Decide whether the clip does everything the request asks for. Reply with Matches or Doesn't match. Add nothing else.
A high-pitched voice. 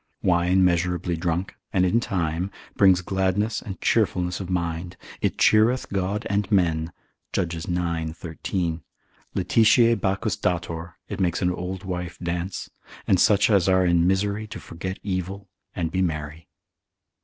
Doesn't match